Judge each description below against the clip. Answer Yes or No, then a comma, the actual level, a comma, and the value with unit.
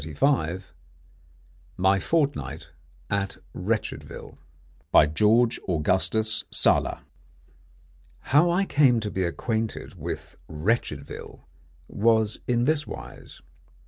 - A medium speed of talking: No, slow, 85 wpm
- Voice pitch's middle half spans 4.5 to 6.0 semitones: Yes, average, 5.2 semitones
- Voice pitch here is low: Yes, low, 110 Hz